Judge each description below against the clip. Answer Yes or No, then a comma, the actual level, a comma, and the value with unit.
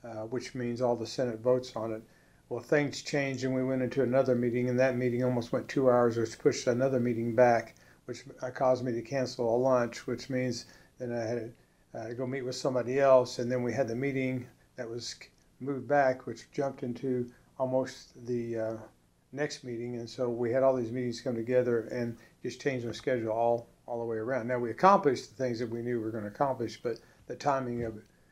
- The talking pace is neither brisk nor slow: No, fast, 225 wpm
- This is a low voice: Yes, low, 125 Hz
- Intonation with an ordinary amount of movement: No, narrow, 1.8 semitones